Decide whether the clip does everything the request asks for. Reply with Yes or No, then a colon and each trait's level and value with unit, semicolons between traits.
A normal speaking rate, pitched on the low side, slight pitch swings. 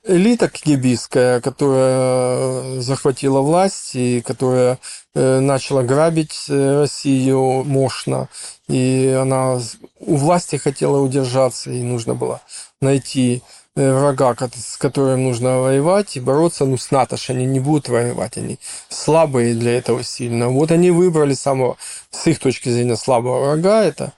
Yes: average, 130 wpm; low, 130 Hz; narrow, 2.2 semitones